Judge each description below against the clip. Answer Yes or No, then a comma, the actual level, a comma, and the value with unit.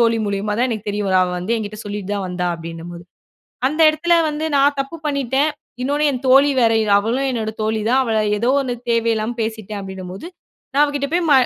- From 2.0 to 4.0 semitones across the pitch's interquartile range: No, average, 5.2 semitones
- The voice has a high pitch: Yes, high, 230 Hz